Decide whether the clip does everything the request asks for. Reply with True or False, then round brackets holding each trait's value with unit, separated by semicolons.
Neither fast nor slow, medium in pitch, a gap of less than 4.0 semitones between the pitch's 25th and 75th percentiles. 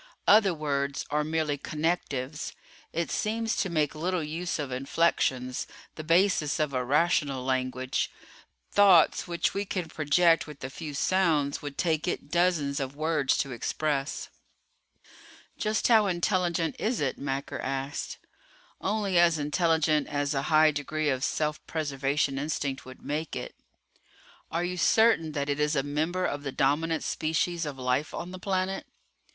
True (150 wpm; 155 Hz; 3.5 semitones)